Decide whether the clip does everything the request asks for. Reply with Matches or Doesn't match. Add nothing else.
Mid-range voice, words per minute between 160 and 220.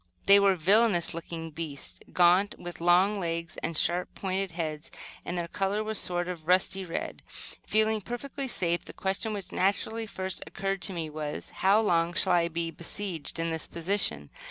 Matches